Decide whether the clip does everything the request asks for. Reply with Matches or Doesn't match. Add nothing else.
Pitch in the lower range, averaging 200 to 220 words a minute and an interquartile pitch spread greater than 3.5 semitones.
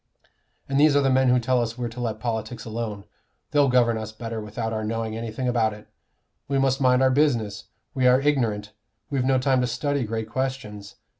Doesn't match